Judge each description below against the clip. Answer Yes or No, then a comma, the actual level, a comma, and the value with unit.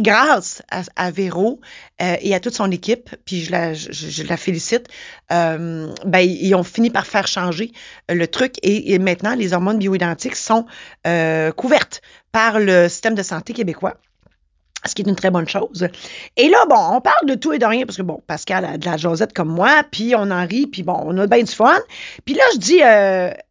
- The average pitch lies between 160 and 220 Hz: Yes, high, 190 Hz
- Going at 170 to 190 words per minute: No, average, 215 wpm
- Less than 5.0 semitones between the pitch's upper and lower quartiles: Yes, average, 4.6 semitones